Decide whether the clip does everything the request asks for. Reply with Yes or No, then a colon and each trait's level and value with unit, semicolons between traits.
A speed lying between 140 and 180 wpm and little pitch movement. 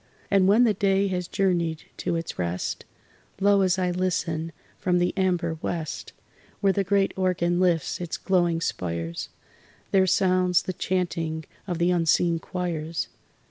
Yes: average, 145 wpm; narrow, 2.2 semitones